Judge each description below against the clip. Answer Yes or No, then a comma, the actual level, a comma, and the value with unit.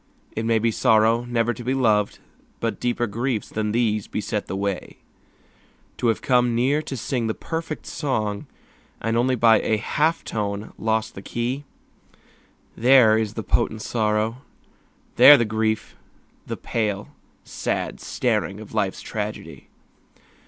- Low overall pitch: Yes, low, 115 Hz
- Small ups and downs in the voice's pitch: Yes, narrow, 2.2 semitones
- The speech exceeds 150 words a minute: No, average, 145 wpm